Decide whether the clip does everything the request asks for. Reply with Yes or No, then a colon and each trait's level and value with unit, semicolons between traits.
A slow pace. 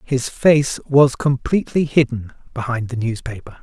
Yes: slow, 130 wpm